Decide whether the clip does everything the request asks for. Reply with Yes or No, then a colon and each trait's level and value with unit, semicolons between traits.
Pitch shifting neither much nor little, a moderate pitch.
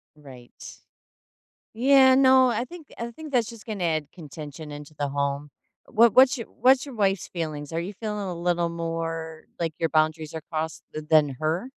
No: wide, 7.1 semitones; medium, 165 Hz